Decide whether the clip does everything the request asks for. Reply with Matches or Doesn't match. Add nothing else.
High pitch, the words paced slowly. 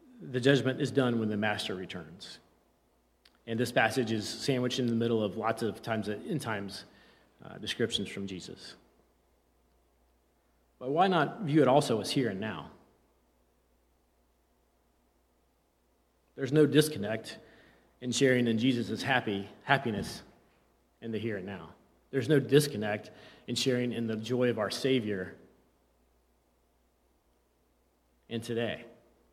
Doesn't match